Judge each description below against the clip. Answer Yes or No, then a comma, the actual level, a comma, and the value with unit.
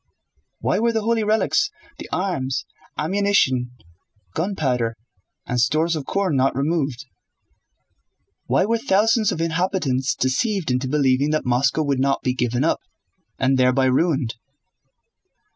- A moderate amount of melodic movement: No, wide, 6.7 semitones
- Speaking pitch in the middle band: Yes, medium, 150 Hz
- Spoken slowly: Yes, slow, 125 wpm